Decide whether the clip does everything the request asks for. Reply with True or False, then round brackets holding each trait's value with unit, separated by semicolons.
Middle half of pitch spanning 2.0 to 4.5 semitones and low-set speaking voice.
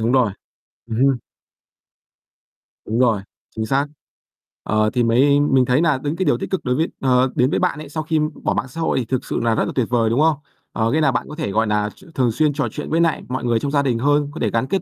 True (4.2 semitones; 130 Hz)